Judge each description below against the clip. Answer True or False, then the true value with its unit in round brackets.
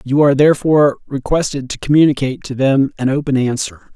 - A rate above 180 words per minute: False (165 wpm)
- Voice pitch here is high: False (140 Hz)